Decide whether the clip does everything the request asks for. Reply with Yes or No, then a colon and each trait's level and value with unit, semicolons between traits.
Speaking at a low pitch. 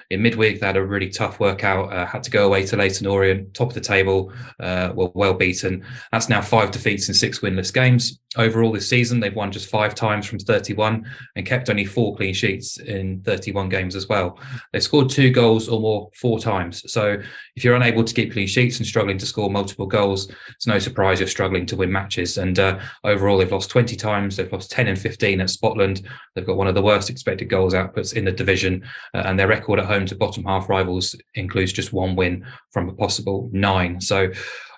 Yes: low, 100 Hz